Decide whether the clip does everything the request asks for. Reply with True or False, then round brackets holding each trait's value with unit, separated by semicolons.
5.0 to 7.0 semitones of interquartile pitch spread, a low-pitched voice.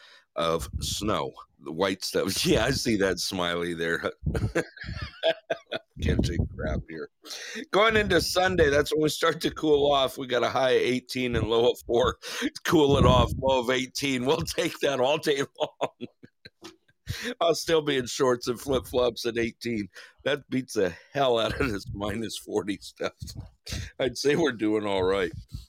True (5.3 semitones; 125 Hz)